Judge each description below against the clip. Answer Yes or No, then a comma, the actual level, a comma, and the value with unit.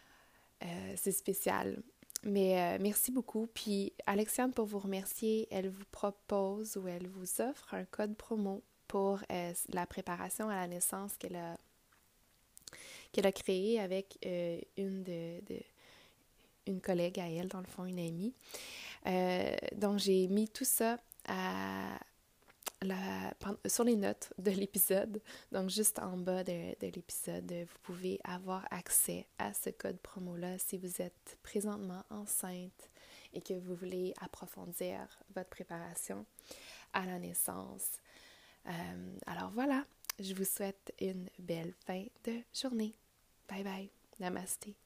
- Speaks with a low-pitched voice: No, high, 190 Hz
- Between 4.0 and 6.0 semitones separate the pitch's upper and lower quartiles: No, narrow, 2.5 semitones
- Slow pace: Yes, slow, 140 wpm